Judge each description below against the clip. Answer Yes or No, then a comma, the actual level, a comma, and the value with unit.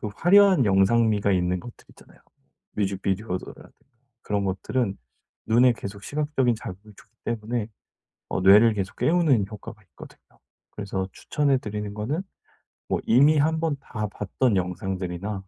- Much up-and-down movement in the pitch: No, average, 4.8 semitones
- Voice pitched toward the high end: No, low, 105 Hz